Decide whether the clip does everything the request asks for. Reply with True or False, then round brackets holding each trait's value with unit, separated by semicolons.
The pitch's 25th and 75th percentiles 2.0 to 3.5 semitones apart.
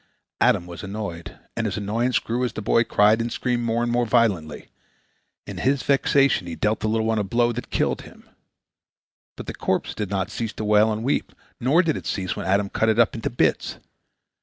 True (2.8 semitones)